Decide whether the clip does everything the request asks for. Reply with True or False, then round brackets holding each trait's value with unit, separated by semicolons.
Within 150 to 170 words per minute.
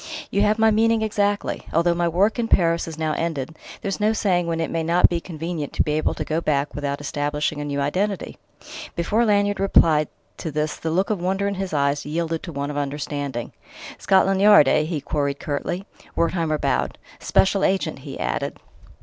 False (200 wpm)